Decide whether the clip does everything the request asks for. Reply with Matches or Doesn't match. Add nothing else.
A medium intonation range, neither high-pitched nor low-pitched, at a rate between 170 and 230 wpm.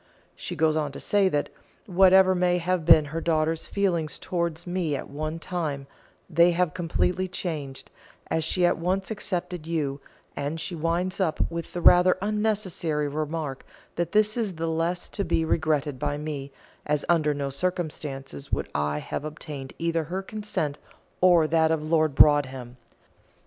Doesn't match